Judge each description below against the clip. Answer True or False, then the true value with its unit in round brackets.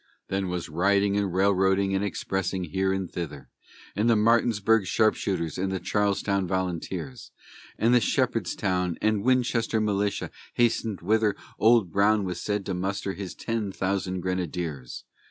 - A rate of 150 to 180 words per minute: False (140 wpm)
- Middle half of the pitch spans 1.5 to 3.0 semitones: True (2.5 semitones)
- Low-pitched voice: True (100 Hz)